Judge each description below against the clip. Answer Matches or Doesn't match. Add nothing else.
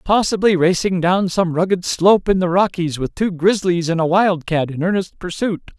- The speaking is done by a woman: Doesn't match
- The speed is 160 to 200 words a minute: Matches